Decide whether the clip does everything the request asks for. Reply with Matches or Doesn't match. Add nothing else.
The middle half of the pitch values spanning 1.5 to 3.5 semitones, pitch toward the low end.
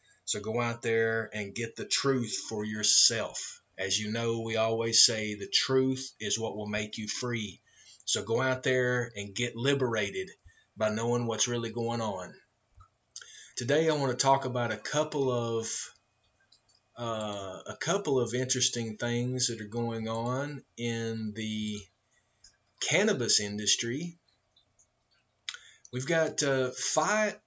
Matches